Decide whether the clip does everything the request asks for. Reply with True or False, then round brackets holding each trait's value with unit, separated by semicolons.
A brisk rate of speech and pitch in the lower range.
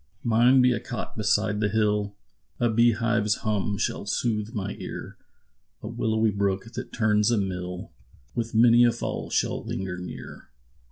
False (160 wpm; 110 Hz)